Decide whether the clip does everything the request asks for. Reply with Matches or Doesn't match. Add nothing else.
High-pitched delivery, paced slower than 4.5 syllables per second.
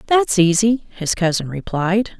Matches